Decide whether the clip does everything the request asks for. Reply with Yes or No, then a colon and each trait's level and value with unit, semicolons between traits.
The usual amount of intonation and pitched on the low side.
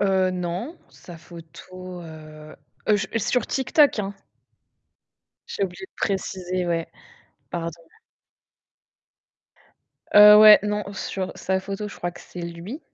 No: average, 3.1 semitones; medium, 185 Hz